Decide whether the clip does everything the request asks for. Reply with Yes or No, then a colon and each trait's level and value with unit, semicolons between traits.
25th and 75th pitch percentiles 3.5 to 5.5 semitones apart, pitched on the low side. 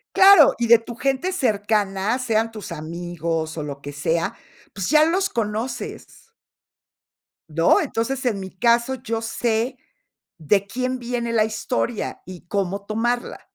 No: average, 4.6 semitones; high, 225 Hz